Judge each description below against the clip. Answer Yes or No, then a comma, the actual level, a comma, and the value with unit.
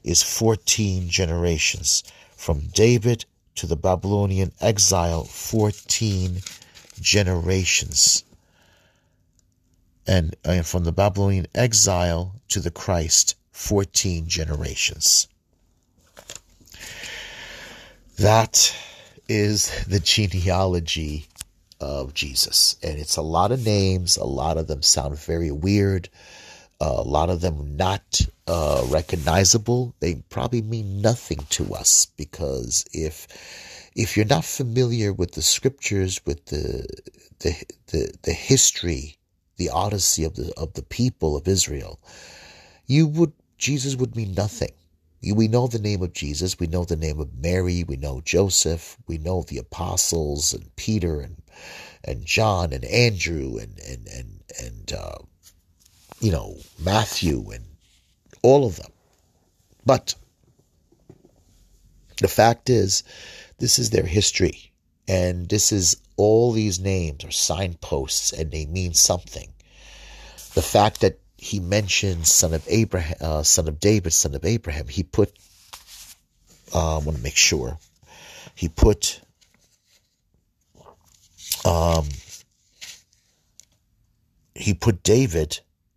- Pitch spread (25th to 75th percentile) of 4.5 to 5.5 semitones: No, average, 4.0 semitones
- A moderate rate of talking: No, slow, 120 wpm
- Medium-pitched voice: No, very low, 90 Hz